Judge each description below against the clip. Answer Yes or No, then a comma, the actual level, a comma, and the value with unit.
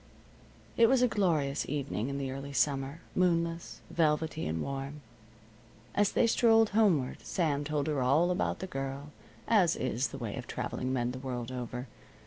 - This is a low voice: No, medium, 145 Hz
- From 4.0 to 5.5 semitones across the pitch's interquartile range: Yes, average, 4.5 semitones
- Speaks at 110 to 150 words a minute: No, average, 165 wpm